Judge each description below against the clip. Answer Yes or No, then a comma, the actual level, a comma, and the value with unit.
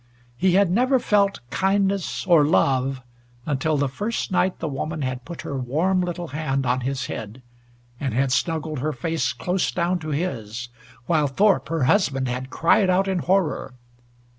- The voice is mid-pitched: Yes, medium, 155 Hz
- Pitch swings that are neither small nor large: No, wide, 5.8 semitones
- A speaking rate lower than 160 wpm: No, average, 165 wpm